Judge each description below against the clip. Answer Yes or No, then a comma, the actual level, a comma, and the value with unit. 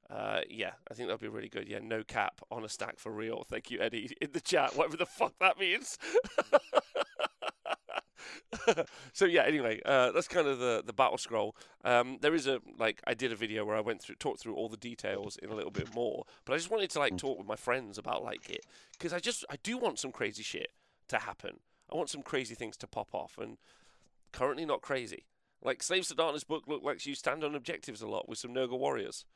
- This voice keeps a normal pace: No, fast, 235 wpm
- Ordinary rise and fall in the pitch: No, wide, 7.2 semitones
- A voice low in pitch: No, medium, 145 Hz